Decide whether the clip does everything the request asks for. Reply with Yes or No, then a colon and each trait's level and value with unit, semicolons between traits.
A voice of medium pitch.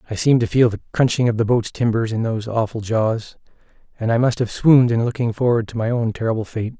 No: low, 115 Hz